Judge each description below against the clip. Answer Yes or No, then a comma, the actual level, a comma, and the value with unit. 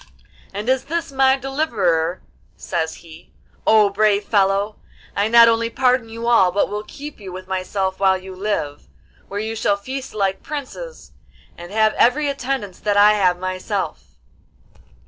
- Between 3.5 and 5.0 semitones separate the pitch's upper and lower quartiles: Yes, average, 4.7 semitones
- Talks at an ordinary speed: Yes, average, 155 wpm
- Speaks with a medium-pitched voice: No, high, 210 Hz